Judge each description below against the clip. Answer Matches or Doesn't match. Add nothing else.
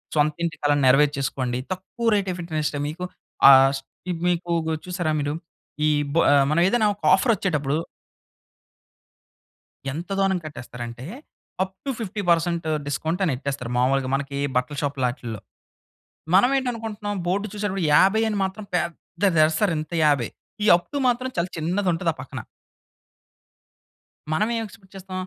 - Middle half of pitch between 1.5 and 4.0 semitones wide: Doesn't match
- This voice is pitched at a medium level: Matches